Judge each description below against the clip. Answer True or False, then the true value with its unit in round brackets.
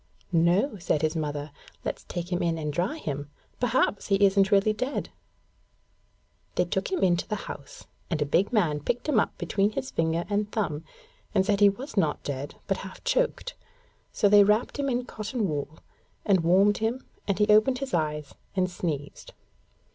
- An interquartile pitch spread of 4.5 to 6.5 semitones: True (4.9 semitones)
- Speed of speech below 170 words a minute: False (180 wpm)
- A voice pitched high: True (195 Hz)